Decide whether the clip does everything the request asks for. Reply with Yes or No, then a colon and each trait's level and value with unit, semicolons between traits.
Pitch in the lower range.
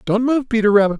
No: high, 225 Hz